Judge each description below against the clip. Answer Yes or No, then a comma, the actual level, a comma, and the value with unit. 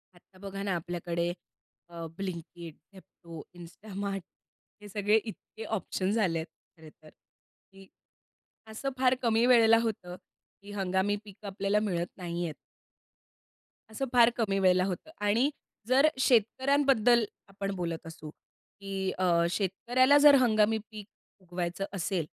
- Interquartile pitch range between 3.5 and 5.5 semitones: Yes, average, 3.9 semitones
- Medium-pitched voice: No, high, 195 Hz